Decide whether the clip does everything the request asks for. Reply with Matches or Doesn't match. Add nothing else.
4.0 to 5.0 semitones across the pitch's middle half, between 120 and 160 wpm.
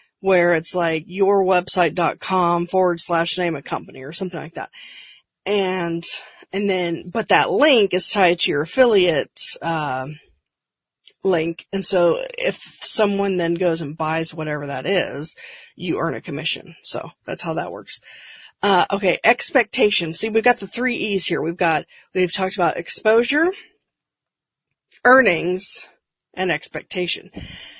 Matches